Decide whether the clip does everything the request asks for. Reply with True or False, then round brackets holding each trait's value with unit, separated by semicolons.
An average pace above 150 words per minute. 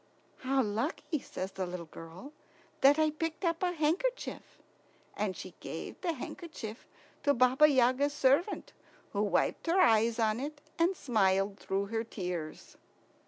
False (145 wpm)